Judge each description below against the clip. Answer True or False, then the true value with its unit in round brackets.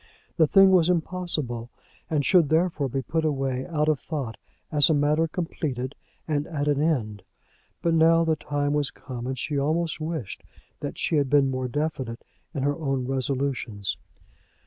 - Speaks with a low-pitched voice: False (145 Hz)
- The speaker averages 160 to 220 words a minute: True (170 wpm)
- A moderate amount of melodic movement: True (3.3 semitones)